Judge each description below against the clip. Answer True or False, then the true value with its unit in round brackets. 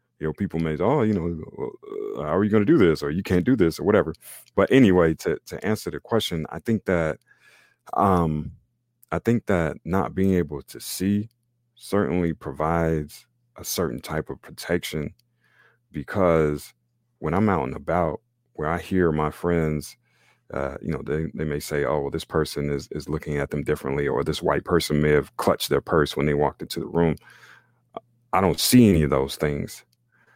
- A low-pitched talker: True (85 Hz)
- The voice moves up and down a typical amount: False (6.1 semitones)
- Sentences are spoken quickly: False (190 wpm)